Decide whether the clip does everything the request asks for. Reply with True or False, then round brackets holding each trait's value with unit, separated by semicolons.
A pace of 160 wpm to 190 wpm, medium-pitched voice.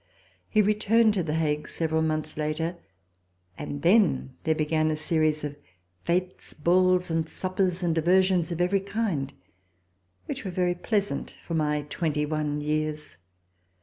False (145 wpm; 160 Hz)